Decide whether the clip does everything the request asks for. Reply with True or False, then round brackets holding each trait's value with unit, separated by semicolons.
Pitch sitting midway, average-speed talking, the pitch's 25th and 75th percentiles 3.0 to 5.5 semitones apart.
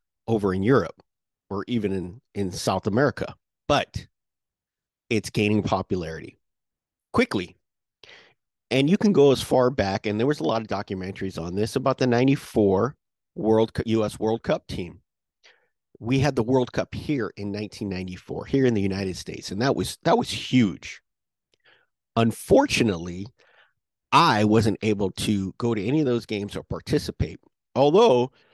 False (110 Hz; 150 wpm; 4.0 semitones)